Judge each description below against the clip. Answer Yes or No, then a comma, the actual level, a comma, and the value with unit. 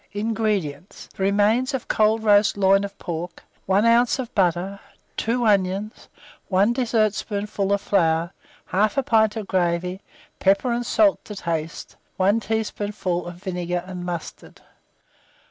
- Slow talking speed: Yes, slow, 130 wpm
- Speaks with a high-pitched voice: Yes, high, 200 Hz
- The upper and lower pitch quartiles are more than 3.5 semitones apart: No, average, 3.2 semitones